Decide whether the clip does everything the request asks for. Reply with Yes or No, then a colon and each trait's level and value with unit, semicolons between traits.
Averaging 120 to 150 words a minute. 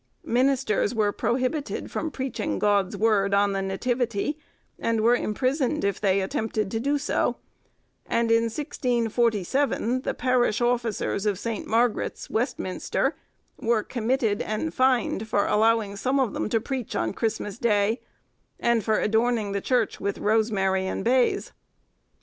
Yes: average, 140 wpm